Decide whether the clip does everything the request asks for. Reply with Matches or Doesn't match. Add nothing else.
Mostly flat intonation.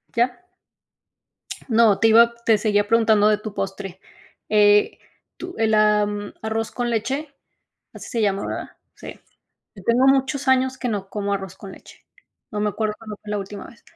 Matches